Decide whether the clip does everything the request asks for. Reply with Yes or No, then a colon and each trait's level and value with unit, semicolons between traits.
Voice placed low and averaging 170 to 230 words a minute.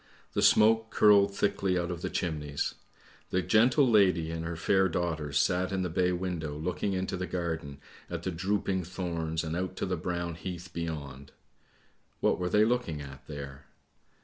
Yes: very low, 90 Hz; average, 175 wpm